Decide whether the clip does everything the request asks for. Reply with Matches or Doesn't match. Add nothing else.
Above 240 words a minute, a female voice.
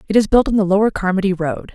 Matches